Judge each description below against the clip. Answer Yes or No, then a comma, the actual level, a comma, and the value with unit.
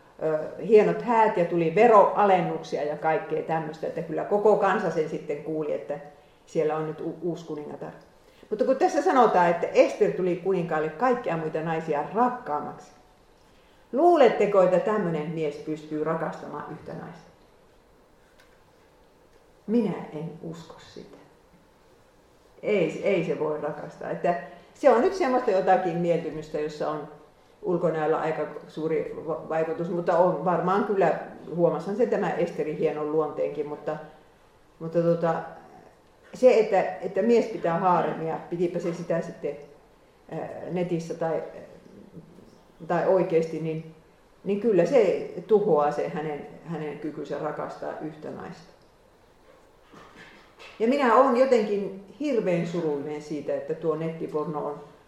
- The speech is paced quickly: No, average, 125 wpm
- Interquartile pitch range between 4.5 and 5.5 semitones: Yes, average, 5.0 semitones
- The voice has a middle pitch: Yes, medium, 170 Hz